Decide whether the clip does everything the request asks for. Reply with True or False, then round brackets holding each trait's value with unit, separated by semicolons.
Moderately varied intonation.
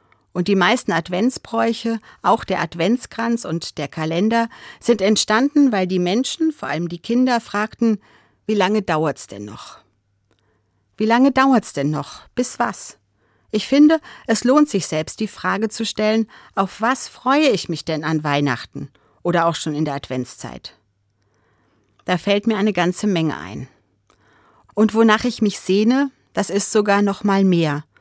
False (6.6 semitones)